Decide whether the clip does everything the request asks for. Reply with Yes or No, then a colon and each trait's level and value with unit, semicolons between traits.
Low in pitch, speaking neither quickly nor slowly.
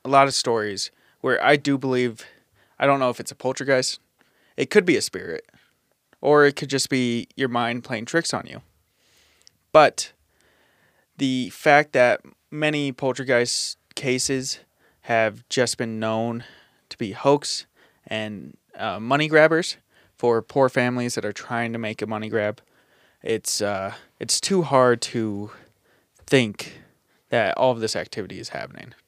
Yes: low, 125 Hz; average, 150 wpm